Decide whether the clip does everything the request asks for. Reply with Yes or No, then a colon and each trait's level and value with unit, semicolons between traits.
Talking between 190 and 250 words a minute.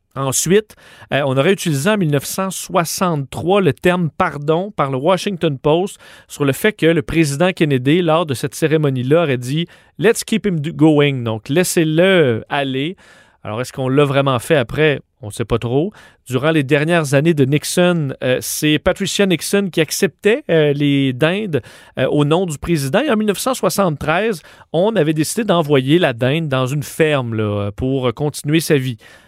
No: average, 170 wpm